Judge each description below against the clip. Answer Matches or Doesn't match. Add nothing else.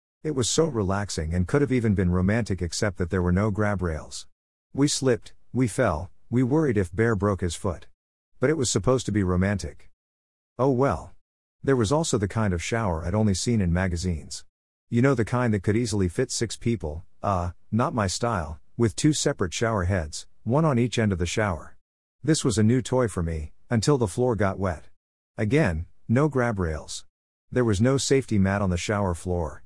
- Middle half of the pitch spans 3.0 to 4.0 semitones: Doesn't match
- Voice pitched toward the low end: Matches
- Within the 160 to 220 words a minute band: Matches